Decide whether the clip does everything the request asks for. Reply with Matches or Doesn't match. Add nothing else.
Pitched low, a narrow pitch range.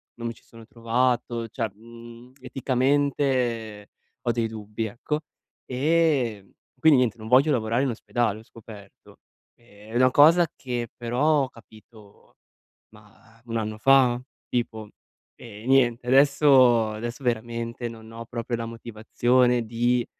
Matches